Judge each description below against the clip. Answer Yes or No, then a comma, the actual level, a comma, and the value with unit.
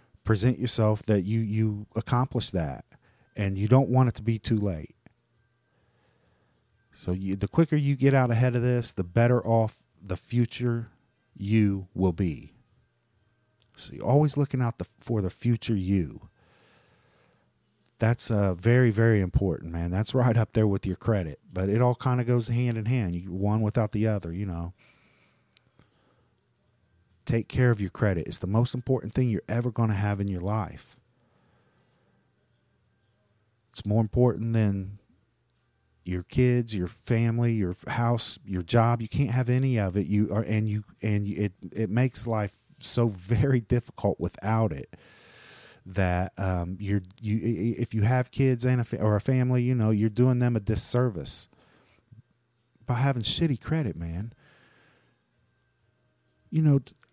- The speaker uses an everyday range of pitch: Yes, average, 3.4 semitones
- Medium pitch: No, low, 110 Hz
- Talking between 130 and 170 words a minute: Yes, average, 160 wpm